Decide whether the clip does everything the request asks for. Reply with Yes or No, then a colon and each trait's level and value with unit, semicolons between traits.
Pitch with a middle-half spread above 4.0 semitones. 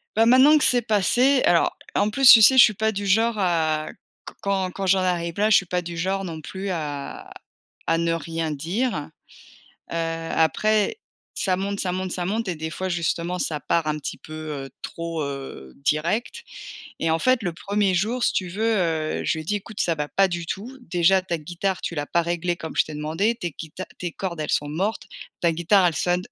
No: average, 3.6 semitones